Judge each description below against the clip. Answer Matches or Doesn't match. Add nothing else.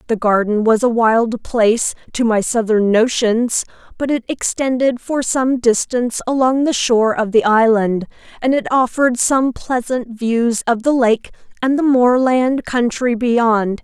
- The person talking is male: Doesn't match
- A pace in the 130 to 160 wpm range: Matches